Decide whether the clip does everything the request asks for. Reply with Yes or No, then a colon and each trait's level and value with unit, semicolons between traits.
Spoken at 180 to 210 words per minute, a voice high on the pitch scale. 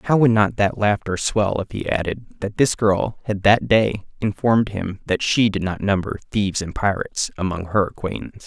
No: average, 200 wpm; low, 105 Hz